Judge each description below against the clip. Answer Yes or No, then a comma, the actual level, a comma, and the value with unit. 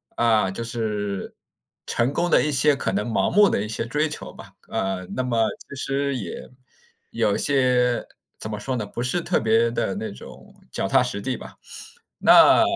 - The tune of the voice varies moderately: Yes, average, 4.2 semitones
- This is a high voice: No, low, 115 Hz